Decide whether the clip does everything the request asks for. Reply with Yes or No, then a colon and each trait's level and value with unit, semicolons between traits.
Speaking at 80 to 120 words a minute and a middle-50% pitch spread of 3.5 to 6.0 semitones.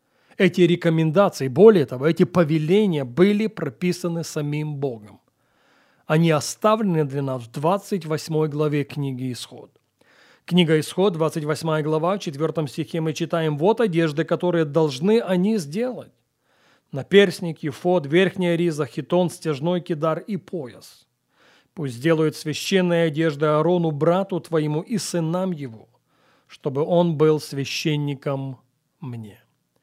No: average, 115 wpm; average, 3.0 semitones